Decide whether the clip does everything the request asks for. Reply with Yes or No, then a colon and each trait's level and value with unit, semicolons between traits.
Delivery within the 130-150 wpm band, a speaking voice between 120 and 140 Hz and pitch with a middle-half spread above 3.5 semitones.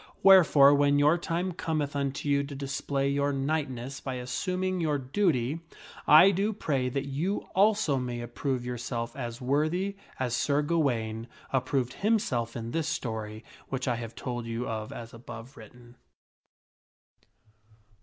Yes: average, 145 wpm; low, 135 Hz; average, 4.3 semitones